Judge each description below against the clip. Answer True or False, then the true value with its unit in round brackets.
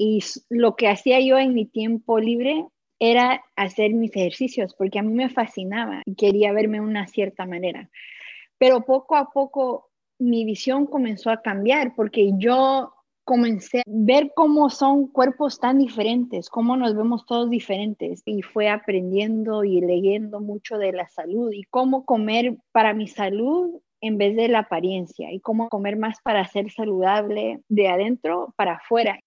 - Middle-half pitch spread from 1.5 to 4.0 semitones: True (3.6 semitones)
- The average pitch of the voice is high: True (225 Hz)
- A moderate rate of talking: True (165 wpm)